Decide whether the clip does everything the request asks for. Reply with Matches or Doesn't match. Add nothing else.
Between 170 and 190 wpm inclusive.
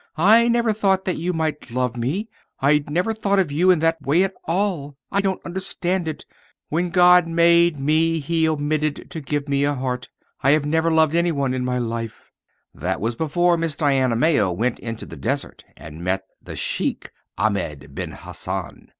Matches